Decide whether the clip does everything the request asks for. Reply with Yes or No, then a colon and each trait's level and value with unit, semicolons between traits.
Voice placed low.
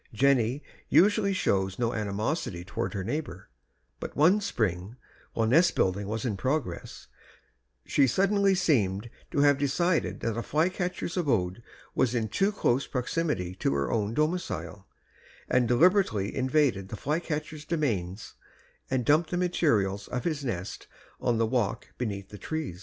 Yes: low, 125 Hz